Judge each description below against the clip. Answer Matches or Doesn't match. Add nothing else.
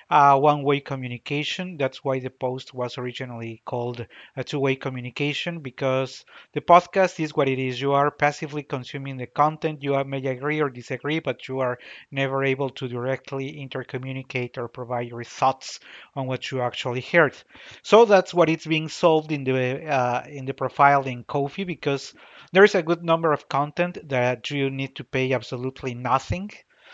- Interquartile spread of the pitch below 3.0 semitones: Matches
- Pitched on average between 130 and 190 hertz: Matches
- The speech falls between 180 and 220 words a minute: Doesn't match